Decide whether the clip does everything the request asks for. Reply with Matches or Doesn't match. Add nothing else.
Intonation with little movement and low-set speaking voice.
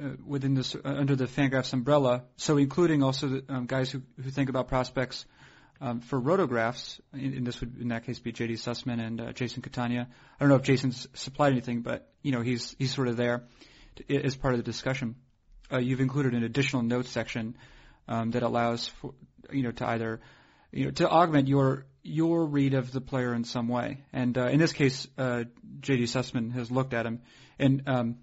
Matches